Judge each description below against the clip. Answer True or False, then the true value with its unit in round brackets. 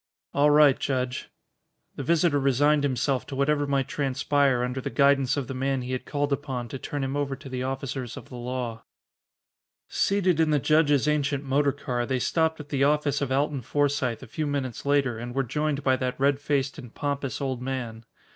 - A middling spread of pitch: False (2.0 semitones)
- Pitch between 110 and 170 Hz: True (140 Hz)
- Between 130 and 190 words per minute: False (200 wpm)